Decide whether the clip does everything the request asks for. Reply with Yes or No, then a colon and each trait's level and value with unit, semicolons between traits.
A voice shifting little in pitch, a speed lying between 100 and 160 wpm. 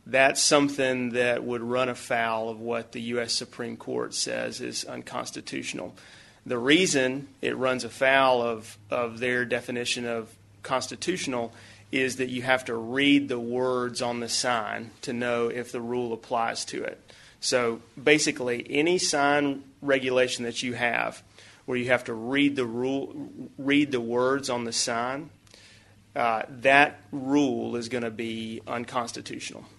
Yes: narrow, 2.3 semitones; average, 150 wpm